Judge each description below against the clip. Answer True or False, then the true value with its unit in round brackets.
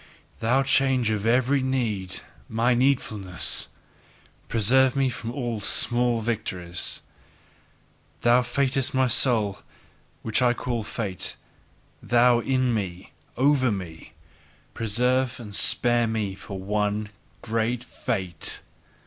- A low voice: True (120 Hz)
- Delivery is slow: True (110 wpm)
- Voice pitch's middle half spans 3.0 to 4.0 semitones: True (3.3 semitones)